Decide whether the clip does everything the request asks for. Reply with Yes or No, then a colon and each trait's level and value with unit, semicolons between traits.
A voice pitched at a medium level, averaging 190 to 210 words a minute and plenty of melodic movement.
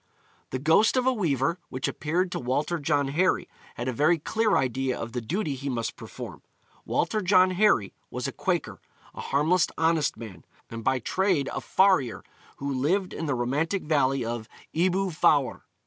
No: medium, 150 Hz; average, 180 wpm; wide, 5.9 semitones